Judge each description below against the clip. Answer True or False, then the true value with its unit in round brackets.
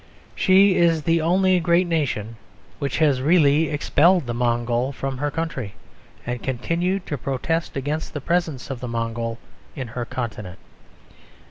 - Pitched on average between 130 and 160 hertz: True (140 Hz)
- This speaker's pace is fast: False (145 wpm)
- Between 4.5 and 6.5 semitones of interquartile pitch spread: True (5.5 semitones)